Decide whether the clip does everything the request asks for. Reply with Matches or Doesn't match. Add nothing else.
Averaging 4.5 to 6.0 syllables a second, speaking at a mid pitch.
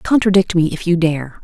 Matches